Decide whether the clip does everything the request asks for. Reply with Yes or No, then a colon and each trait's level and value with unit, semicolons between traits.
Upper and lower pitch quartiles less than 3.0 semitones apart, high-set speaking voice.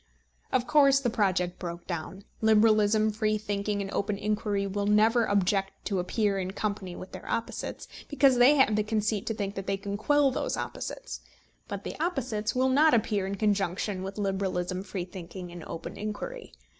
Yes: narrow, 2.4 semitones; high, 205 Hz